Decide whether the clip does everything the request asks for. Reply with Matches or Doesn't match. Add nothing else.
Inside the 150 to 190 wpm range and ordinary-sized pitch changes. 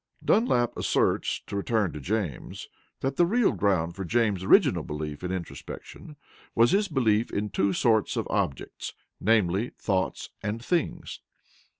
Doesn't match